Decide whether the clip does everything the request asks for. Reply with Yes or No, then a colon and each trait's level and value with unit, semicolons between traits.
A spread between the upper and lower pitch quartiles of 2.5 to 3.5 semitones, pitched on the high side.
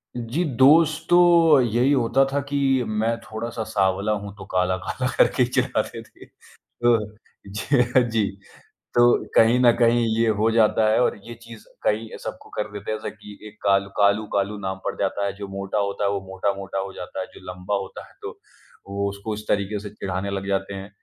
No: average, 3.2 semitones; low, 105 Hz